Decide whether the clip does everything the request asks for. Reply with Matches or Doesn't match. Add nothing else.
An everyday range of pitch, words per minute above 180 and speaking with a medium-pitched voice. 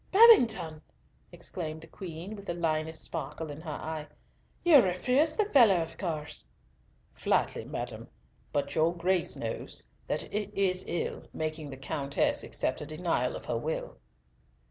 Doesn't match